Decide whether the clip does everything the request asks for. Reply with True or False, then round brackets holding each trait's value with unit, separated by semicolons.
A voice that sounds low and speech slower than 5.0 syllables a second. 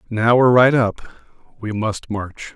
True (115 Hz; 4.6 syllables/s)